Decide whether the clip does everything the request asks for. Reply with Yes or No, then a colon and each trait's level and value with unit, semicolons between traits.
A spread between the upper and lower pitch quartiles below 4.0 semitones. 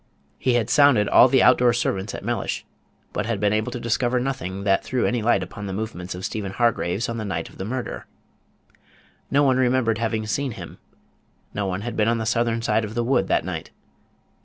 Yes: average, 2.8 semitones